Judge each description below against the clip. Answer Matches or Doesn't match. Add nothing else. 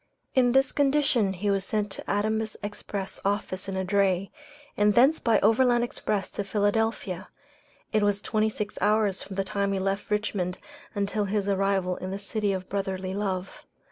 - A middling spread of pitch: Doesn't match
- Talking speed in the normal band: Matches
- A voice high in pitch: Matches